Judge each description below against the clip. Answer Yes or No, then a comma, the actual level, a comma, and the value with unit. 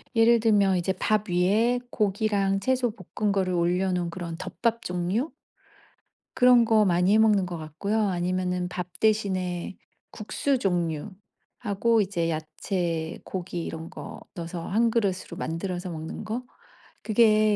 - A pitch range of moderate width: Yes, average, 3.5 semitones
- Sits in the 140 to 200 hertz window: Yes, high, 190 Hz